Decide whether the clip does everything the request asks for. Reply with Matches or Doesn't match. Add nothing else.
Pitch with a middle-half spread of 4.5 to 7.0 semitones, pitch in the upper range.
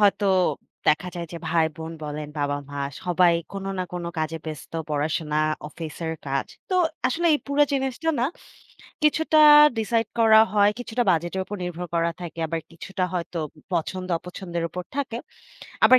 Doesn't match